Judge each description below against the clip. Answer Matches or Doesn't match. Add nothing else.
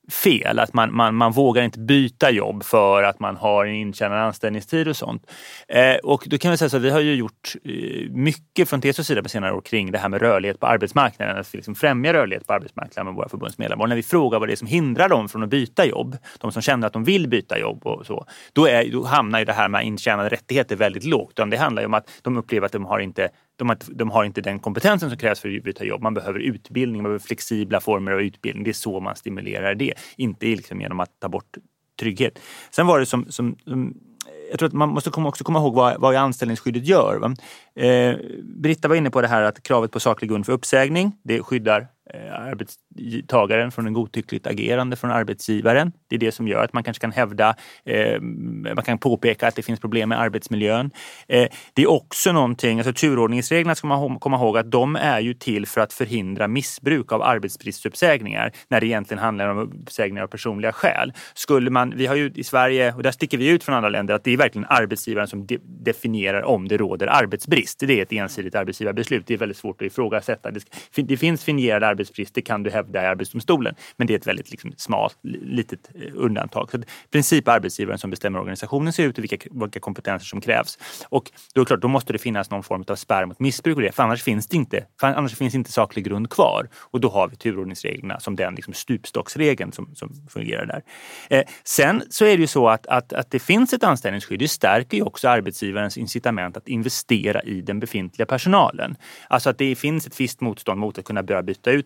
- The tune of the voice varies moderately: Matches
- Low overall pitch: Matches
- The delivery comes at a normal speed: Doesn't match